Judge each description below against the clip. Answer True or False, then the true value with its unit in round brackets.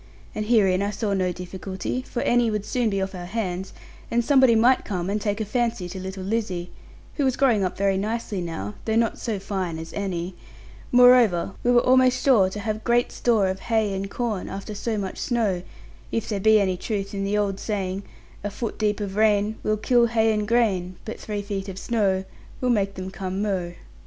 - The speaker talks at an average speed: False (210 wpm)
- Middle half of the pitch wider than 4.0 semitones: False (3.1 semitones)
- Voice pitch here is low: False (205 Hz)